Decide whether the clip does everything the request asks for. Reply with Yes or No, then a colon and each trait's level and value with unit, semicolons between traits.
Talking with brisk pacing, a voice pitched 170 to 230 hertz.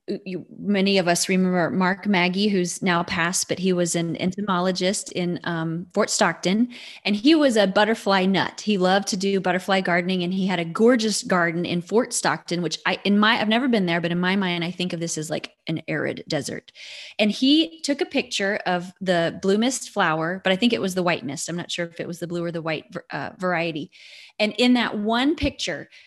Yes: fast, 225 wpm; medium, 185 Hz